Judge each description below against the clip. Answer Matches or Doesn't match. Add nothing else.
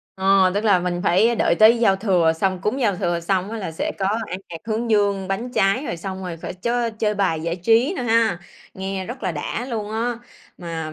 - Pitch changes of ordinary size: Matches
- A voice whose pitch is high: Matches